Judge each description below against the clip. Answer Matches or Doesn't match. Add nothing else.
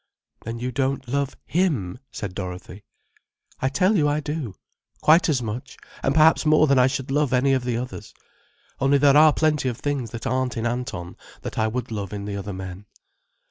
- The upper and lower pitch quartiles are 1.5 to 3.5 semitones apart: Doesn't match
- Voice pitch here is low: Matches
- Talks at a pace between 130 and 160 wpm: Doesn't match